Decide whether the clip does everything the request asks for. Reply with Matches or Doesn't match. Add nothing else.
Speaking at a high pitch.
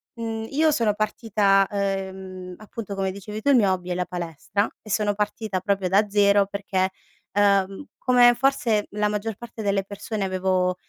Matches